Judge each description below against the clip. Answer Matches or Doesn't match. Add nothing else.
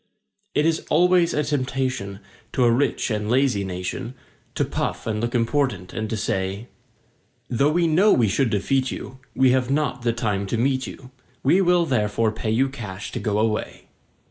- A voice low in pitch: Matches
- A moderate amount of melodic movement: Matches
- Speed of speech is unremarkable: Matches